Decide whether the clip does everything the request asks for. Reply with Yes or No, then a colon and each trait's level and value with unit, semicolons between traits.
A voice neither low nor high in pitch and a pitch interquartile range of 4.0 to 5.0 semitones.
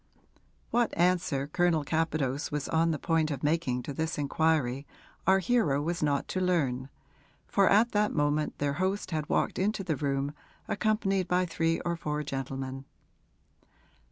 Yes: medium, 160 Hz; average, 4.3 semitones